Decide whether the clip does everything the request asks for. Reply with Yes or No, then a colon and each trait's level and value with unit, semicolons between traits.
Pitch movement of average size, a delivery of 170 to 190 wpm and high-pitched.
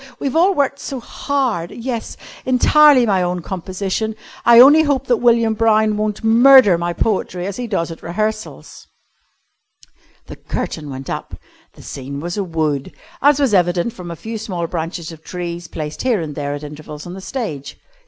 No: wide, 6.0 semitones; average, 175 wpm; high, 200 Hz